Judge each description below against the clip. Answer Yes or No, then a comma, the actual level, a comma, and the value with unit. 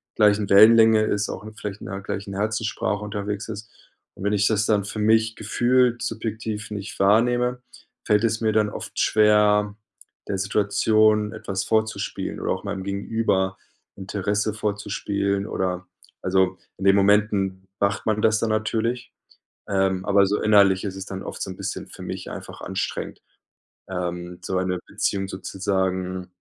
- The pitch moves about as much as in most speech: No, narrow, 1.9 semitones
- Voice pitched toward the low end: Yes, low, 105 Hz